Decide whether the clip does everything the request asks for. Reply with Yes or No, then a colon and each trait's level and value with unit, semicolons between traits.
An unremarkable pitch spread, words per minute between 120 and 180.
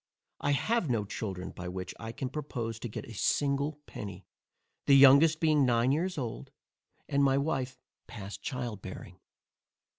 Yes: average, 4.9 semitones; average, 155 wpm